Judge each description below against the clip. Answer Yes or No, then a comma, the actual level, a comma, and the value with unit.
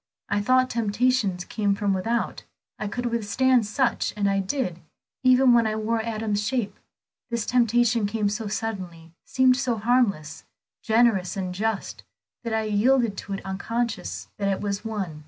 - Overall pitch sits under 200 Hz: No, high, 220 Hz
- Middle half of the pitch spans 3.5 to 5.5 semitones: No, average, 3.0 semitones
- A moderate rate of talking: Yes, average, 155 wpm